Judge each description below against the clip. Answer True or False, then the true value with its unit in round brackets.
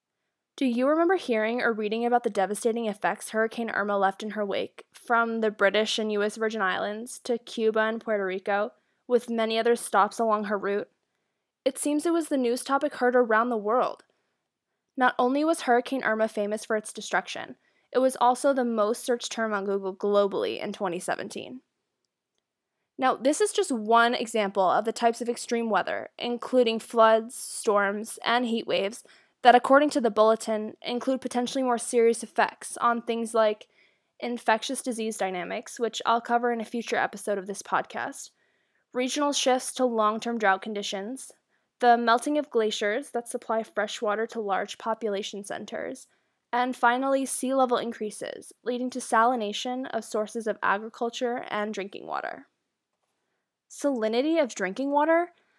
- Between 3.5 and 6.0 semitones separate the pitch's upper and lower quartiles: False (2.7 semitones)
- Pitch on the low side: False (230 Hz)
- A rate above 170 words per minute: False (160 wpm)